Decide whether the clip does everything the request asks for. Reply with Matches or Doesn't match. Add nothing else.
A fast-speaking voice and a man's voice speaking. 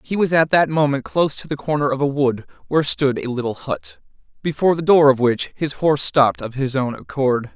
Matches